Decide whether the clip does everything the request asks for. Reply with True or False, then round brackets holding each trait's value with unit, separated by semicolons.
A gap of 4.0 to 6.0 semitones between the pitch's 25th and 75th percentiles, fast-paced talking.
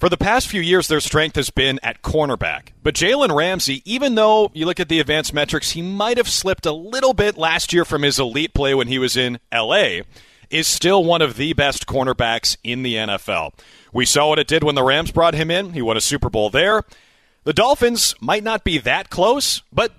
True (5.6 semitones; 225 wpm)